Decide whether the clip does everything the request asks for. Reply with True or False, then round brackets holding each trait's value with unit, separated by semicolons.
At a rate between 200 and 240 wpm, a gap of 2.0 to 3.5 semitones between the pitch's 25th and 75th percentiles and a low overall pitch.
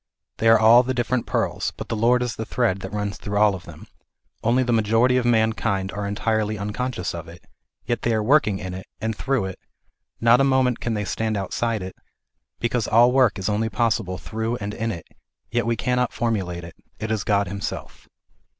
True (205 wpm; 2.9 semitones; 110 Hz)